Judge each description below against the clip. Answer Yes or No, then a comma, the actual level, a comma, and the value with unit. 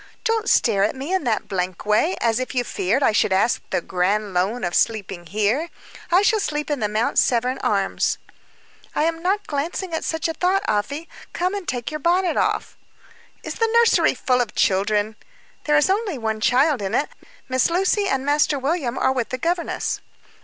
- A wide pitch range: Yes, wide, 7.9 semitones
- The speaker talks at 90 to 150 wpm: No, average, 195 wpm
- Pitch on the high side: Yes, very high, 265 Hz